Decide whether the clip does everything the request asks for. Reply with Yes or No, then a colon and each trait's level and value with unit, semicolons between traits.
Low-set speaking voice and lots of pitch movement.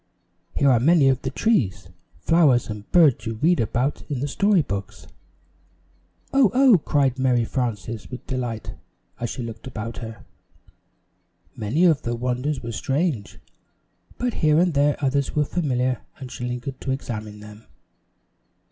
No: low, 130 Hz; average, 4.3 semitones